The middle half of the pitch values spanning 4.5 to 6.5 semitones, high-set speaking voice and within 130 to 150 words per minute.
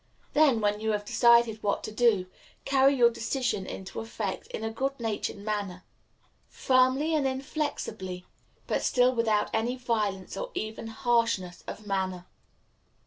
No: average, 3.7 semitones; high, 225 Hz; average, 140 wpm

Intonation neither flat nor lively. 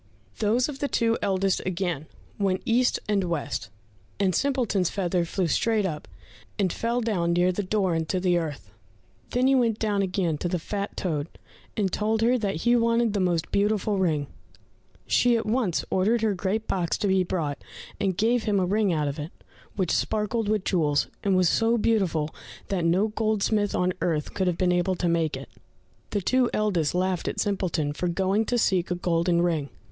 Yes: average, 3.9 semitones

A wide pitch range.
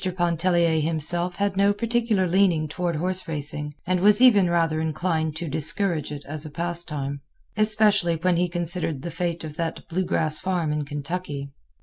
No: average, 3.0 semitones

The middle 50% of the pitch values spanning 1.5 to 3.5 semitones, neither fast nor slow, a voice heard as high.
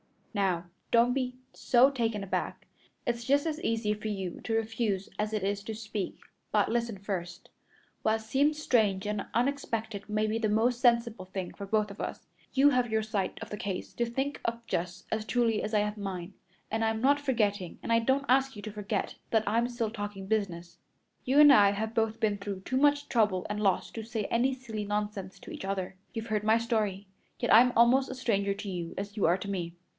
No: average, 2.9 semitones; fast, 210 wpm; high, 220 Hz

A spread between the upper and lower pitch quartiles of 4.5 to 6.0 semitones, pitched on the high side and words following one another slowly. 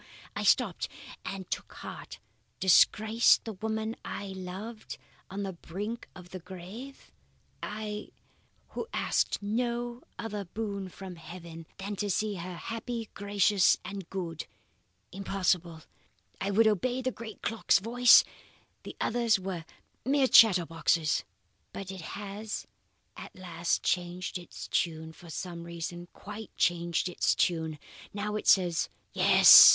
No: average, 3.7 semitones; high, 195 Hz; slow, 130 wpm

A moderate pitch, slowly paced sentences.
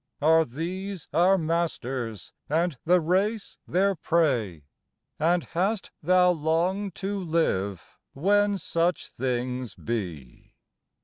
Yes: medium, 165 Hz; slow, 105 wpm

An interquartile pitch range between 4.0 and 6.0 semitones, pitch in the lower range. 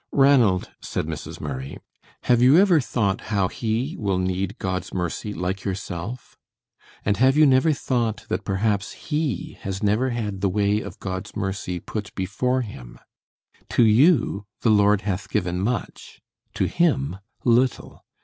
Yes: average, 4.8 semitones; low, 105 Hz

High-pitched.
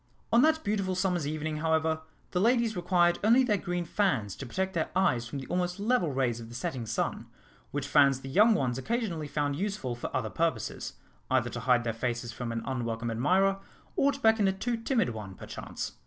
No: medium, 160 Hz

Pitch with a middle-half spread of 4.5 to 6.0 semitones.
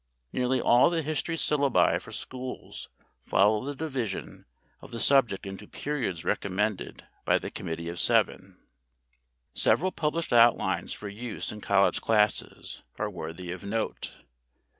Yes: wide, 5.6 semitones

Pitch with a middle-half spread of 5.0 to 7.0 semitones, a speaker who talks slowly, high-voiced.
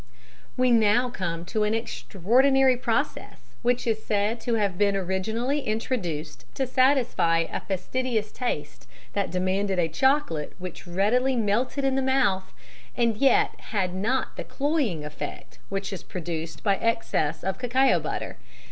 No: wide, 5.5 semitones; average, 145 wpm; high, 215 Hz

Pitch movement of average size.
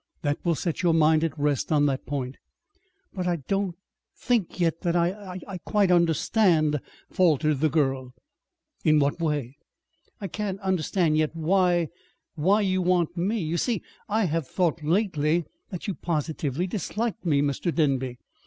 Yes: average, 3.8 semitones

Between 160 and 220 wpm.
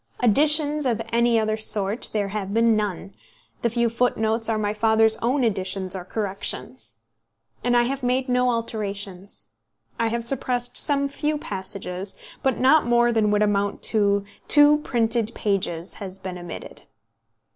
No: average, 150 wpm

